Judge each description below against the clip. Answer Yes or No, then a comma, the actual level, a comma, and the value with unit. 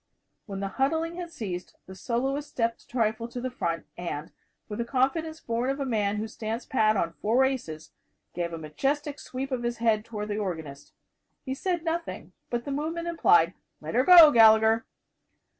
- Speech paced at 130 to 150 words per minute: No, average, 185 wpm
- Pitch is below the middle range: No, high, 235 Hz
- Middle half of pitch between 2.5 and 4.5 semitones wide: No, average, 5.0 semitones